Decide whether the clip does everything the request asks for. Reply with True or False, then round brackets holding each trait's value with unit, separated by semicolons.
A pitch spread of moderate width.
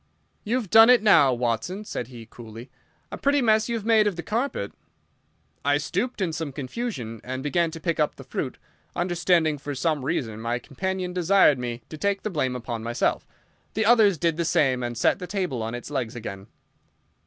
False (8.1 semitones)